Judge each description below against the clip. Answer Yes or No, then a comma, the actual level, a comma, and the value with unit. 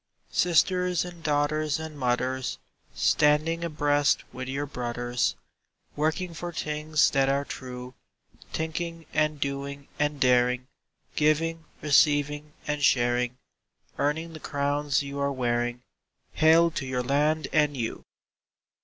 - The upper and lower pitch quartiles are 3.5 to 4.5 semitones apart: No, average, 3.1 semitones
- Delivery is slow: Yes, slow, 120 wpm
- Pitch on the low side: No, medium, 145 Hz